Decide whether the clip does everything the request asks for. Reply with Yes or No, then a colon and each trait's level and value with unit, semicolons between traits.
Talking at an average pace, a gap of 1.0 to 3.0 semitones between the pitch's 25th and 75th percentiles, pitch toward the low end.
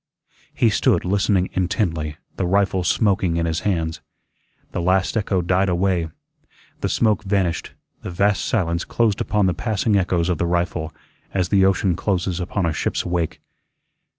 Yes: average, 155 wpm; narrow, 2.4 semitones; very low, 90 Hz